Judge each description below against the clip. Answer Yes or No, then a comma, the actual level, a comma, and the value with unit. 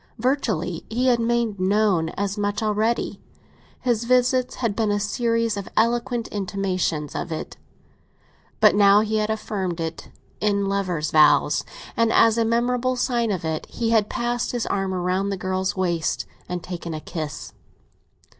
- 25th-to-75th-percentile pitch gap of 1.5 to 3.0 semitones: No, average, 3.9 semitones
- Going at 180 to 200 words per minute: No, average, 155 wpm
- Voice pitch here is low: No, high, 205 Hz